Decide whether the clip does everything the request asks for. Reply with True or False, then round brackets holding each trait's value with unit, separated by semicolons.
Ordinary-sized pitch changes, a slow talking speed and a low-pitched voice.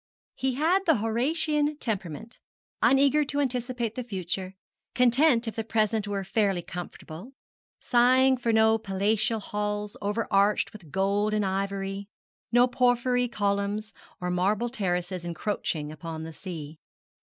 False (4.1 semitones; 130 wpm; 215 Hz)